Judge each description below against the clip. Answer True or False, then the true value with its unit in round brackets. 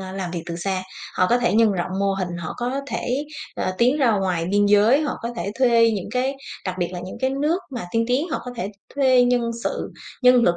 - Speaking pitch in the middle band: False (230 Hz)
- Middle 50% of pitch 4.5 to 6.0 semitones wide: True (5.1 semitones)